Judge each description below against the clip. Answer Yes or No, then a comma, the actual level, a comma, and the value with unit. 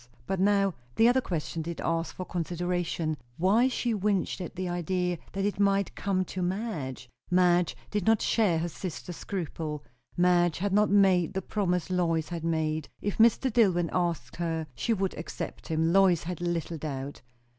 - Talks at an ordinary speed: Yes, average, 170 wpm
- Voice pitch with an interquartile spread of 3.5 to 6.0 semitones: No, average, 3.0 semitones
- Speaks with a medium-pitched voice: Yes, medium, 180 Hz